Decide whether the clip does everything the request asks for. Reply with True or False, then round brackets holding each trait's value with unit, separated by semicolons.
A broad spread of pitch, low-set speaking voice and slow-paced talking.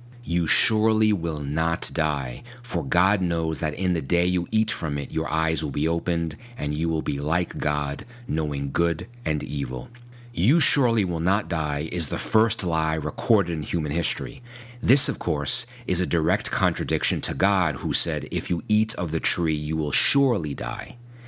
False (5.8 semitones; 85 Hz; 185 wpm)